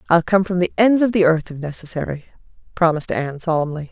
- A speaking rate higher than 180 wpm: Yes, average, 200 wpm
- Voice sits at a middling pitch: Yes, medium, 170 Hz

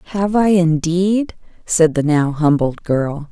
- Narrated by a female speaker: Yes, female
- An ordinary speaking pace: Yes, average, 145 wpm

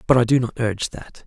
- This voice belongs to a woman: No, male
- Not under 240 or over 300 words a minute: Yes, fast, 285 wpm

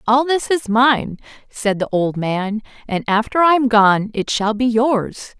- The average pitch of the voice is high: Yes, high, 230 Hz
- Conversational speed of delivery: Yes, average, 190 wpm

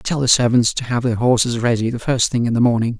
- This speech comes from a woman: No, male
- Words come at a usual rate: No, fast, 280 wpm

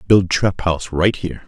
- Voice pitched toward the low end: Yes, very low, 90 Hz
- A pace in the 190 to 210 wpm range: Yes, fast, 205 wpm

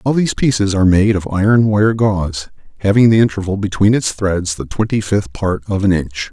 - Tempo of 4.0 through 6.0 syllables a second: Yes, 5.5 syllables/s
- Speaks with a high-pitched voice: No, low, 100 Hz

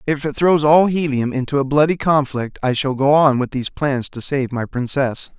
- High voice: No, medium, 140 Hz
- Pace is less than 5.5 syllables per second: Yes, 5.0 syllables/s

